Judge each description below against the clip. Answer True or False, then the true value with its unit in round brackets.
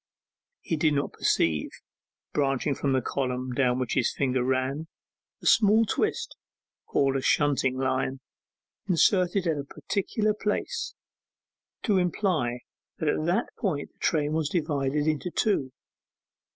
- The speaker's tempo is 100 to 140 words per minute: True (135 wpm)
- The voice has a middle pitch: True (145 Hz)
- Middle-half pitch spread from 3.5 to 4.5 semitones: False (5.2 semitones)